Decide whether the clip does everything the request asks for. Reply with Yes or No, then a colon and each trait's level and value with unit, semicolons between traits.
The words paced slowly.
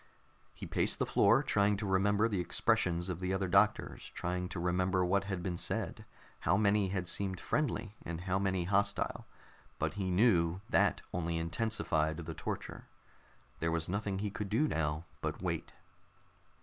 No: average, 165 wpm